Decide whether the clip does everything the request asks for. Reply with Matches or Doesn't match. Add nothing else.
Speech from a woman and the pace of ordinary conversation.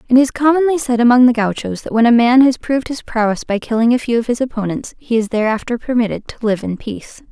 Doesn't match